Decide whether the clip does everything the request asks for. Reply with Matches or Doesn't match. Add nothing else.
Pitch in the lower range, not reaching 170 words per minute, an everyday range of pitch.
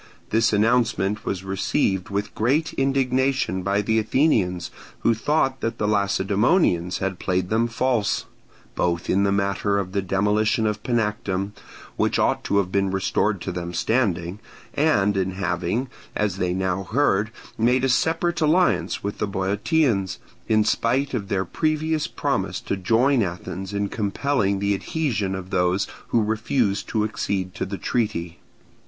Matches